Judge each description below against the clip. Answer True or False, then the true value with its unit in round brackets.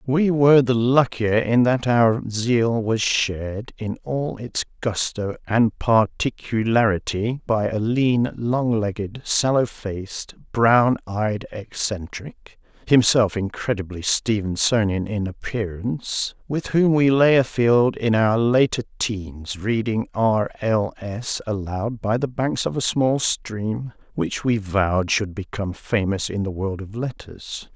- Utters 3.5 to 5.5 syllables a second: False (3.3 syllables/s)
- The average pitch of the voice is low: True (115 Hz)